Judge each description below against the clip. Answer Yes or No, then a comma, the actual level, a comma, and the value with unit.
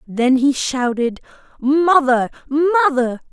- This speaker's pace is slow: Yes, slow, 90 wpm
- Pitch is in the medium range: No, very high, 275 Hz